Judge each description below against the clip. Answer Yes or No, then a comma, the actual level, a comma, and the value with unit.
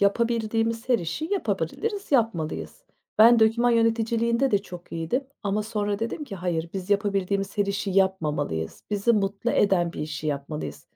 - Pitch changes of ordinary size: Yes, average, 4.5 semitones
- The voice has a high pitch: Yes, high, 205 Hz